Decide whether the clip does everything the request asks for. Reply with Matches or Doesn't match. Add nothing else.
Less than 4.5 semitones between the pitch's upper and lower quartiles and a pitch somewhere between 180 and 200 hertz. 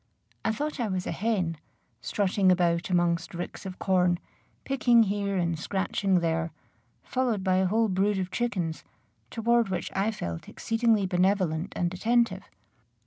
Matches